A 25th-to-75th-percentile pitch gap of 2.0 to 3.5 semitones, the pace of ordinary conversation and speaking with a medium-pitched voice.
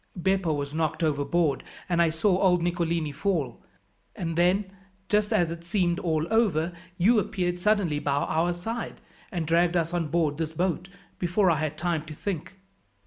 Yes: average, 2.8 semitones; average, 170 wpm; medium, 170 Hz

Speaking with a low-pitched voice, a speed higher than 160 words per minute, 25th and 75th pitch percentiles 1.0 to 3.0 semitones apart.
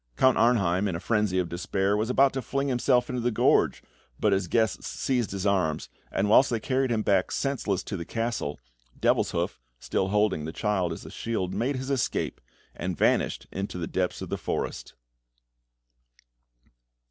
No: low, 105 Hz; average, 175 wpm; average, 4.8 semitones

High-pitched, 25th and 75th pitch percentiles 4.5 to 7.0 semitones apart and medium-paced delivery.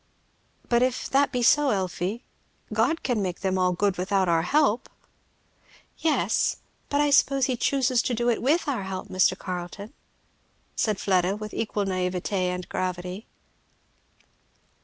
Yes: high, 205 Hz; wide, 5.6 semitones; average, 145 wpm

